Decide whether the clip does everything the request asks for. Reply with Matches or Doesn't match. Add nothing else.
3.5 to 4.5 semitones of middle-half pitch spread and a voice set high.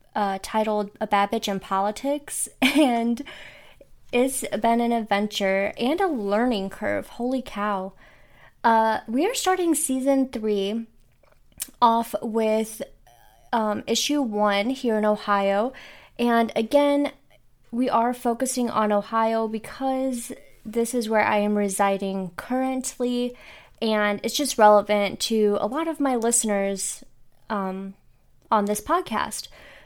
Matches